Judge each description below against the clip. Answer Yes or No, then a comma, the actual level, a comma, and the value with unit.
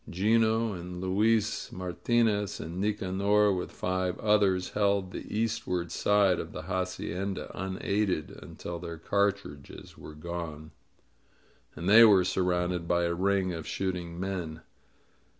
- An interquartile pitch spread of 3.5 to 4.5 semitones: No, average, 2.7 semitones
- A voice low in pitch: Yes, very low, 95 Hz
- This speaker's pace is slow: Yes, slow, 130 wpm